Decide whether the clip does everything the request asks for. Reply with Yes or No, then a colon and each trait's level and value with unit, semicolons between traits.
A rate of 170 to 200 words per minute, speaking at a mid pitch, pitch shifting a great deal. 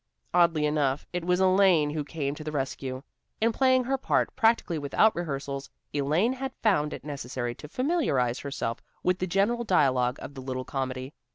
Yes: average, 175 wpm; medium, 150 Hz; wide, 6.1 semitones